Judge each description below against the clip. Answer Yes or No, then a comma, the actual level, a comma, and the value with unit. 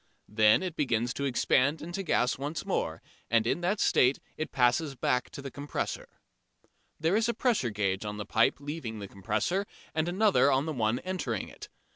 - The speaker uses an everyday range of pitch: No, wide, 6.4 semitones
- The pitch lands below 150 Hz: Yes, medium, 140 Hz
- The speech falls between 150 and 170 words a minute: No, average, 185 wpm